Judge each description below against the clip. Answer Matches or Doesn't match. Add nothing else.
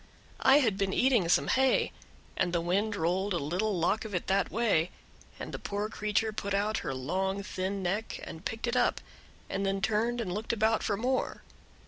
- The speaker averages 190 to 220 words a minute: Matches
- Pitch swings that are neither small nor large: Matches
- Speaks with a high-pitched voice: Matches